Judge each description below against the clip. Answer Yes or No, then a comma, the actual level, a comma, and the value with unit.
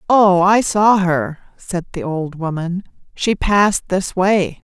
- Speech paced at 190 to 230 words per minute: No, average, 155 wpm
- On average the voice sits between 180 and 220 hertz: Yes, medium, 185 Hz